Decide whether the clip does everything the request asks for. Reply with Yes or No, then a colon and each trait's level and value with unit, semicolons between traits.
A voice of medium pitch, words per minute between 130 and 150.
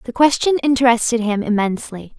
No: high, 240 Hz; slow, 135 wpm